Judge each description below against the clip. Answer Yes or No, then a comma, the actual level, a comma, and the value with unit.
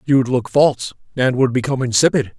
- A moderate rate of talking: Yes, average, 175 wpm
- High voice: No, low, 130 Hz